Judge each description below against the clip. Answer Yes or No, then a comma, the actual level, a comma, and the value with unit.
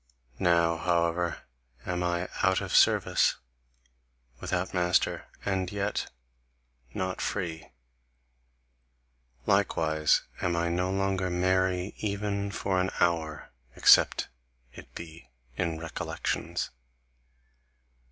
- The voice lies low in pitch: Yes, very low, 90 Hz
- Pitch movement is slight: Yes, narrow, 1.8 semitones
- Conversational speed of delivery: No, slow, 95 wpm